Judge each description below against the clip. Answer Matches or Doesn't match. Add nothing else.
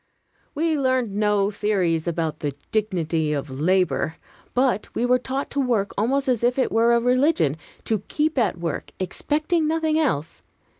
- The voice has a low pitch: Doesn't match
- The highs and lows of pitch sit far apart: Matches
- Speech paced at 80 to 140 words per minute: Doesn't match